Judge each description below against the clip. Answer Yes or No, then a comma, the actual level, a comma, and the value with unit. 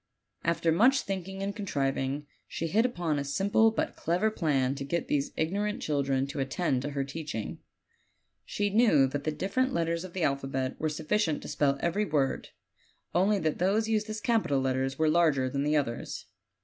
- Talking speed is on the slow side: No, average, 185 wpm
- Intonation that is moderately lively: No, wide, 6.2 semitones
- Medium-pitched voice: Yes, medium, 160 Hz